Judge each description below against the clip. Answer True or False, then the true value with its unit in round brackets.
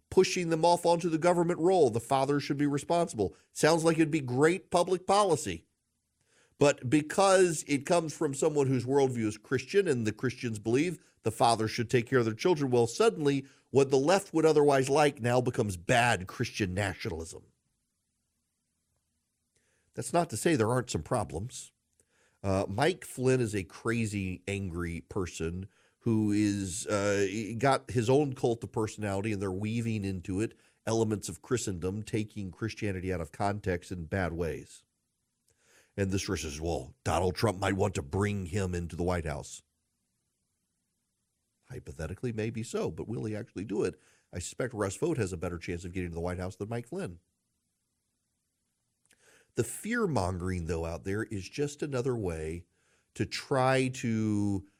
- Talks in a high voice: False (110 Hz)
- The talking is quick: False (165 wpm)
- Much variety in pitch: True (6.5 semitones)